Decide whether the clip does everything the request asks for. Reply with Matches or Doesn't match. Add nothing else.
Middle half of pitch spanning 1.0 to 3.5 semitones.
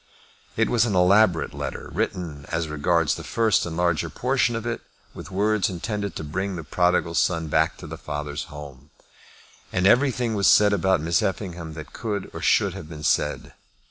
Doesn't match